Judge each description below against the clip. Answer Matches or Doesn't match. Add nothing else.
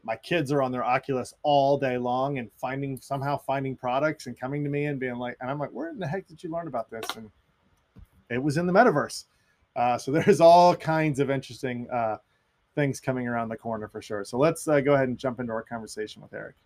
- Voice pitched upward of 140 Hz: Doesn't match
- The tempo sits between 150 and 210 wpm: Doesn't match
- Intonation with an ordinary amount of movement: Matches